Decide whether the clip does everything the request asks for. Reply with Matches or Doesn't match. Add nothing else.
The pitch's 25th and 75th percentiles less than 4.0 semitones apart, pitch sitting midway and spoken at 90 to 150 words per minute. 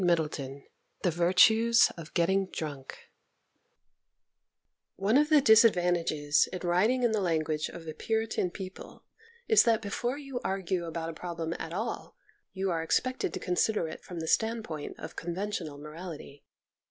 Doesn't match